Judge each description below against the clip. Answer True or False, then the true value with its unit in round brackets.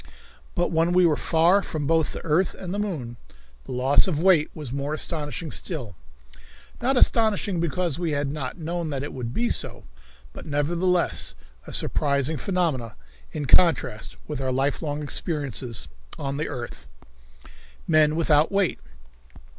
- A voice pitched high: False (155 Hz)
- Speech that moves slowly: False (150 wpm)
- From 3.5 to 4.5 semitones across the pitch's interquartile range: True (3.8 semitones)